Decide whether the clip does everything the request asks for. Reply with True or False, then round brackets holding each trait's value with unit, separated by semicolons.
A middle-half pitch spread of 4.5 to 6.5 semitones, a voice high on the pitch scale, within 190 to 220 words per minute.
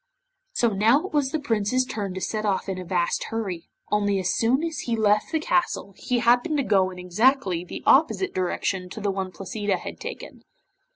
True (5.2 semitones; 210 Hz; 205 wpm)